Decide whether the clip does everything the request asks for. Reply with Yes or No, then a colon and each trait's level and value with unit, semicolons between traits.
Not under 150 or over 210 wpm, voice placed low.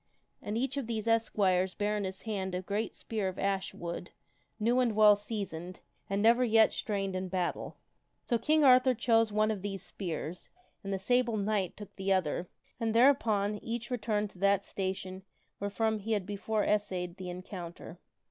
No: average, 180 wpm; high, 205 Hz